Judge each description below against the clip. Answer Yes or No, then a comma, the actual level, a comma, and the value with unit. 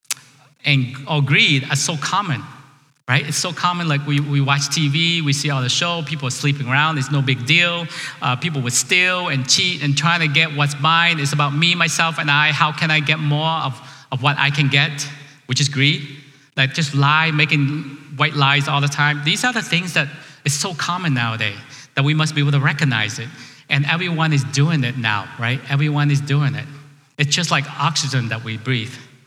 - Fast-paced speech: Yes, fast, 215 wpm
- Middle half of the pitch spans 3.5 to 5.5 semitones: No, narrow, 2.4 semitones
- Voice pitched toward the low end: No, medium, 145 Hz